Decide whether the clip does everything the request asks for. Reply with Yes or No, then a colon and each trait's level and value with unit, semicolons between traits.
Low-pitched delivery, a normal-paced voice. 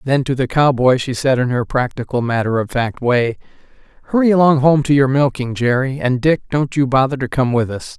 No: low, 130 Hz; fast, 220 wpm